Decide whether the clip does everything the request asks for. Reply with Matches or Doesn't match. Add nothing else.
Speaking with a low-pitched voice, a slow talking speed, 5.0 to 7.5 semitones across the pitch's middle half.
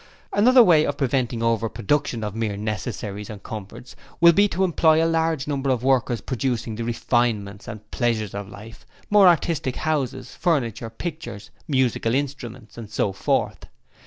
Doesn't match